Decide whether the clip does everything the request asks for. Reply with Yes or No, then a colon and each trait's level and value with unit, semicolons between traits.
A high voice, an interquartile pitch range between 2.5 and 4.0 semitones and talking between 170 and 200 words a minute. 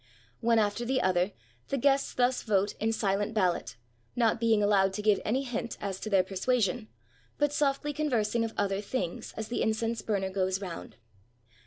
Yes: high, 215 Hz; average, 3.7 semitones; average, 180 wpm